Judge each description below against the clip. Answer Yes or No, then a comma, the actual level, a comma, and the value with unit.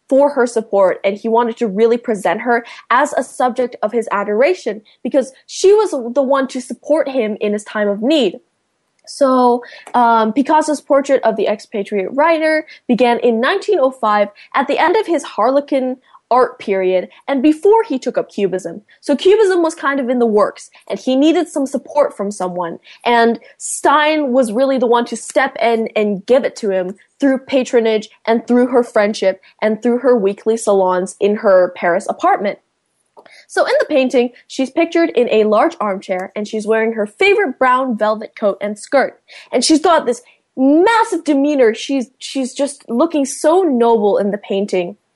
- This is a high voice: Yes, high, 245 Hz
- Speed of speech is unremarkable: Yes, average, 175 wpm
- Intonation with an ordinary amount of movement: Yes, average, 4.9 semitones